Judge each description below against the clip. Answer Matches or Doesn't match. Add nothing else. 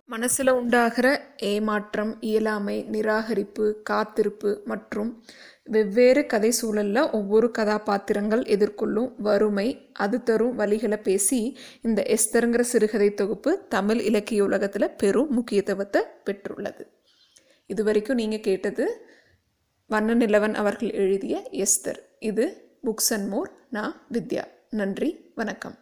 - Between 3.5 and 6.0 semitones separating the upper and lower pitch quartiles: Doesn't match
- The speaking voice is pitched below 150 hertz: Doesn't match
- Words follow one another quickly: Doesn't match